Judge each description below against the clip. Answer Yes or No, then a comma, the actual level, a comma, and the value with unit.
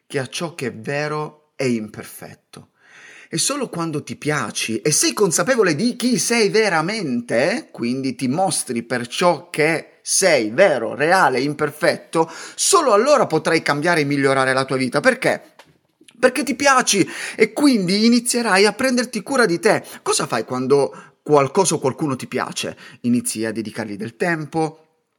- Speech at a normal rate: Yes, average, 150 wpm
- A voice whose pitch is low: No, medium, 160 Hz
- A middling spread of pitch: No, wide, 8.2 semitones